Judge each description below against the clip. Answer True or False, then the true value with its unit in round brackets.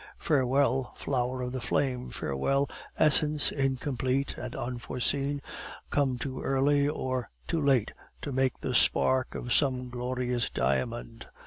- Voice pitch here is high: False (130 Hz)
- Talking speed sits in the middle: False (125 wpm)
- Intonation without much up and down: True (2.0 semitones)